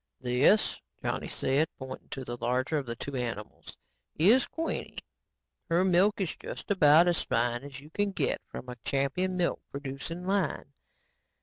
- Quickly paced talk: No, average, 160 wpm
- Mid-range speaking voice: Yes, medium, 145 Hz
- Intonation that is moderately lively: No, wide, 5.9 semitones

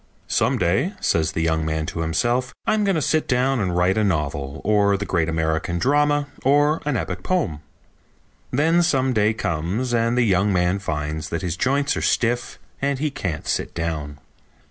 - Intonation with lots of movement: Yes, wide, 8.5 semitones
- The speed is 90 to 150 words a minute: No, average, 185 wpm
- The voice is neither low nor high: No, low, 100 Hz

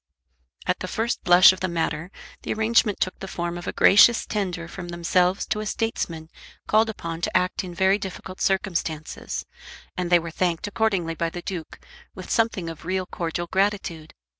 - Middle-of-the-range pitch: Yes, medium, 180 Hz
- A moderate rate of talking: Yes, average, 180 wpm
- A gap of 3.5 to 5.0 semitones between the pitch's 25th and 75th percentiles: No, average, 2.7 semitones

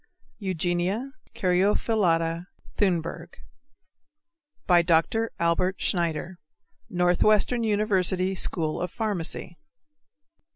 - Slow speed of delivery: Yes, slow, 65 wpm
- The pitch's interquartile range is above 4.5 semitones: No, average, 3.3 semitones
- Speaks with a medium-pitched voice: Yes, medium, 180 Hz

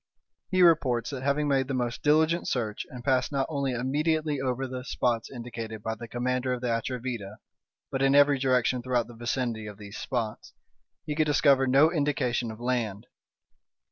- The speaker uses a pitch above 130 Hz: No, low, 125 Hz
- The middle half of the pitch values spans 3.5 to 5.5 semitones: No, average, 2.9 semitones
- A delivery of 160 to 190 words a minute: Yes, average, 175 wpm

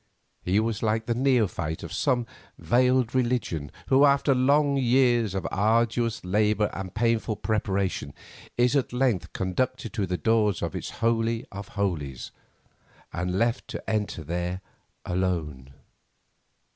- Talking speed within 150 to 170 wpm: No, slow, 135 wpm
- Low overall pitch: Yes, low, 110 Hz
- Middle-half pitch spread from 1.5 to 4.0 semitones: No, average, 4.8 semitones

